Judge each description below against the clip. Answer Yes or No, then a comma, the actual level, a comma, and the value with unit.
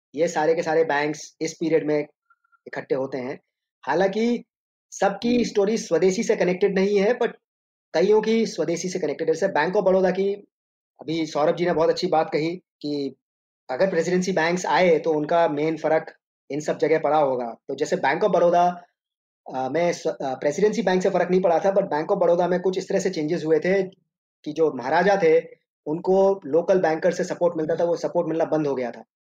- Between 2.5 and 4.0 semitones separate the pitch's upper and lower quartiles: Yes, average, 3.7 semitones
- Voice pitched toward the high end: No, medium, 175 Hz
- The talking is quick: Yes, fast, 195 wpm